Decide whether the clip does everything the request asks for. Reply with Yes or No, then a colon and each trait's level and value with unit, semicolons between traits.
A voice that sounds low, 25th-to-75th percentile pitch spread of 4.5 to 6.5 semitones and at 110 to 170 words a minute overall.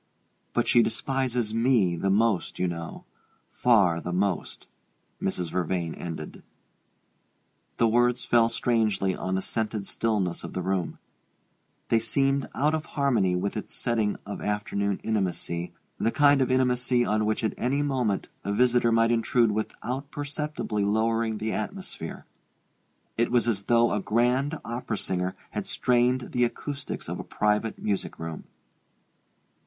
No: low, 115 Hz; average, 3.9 semitones; average, 145 wpm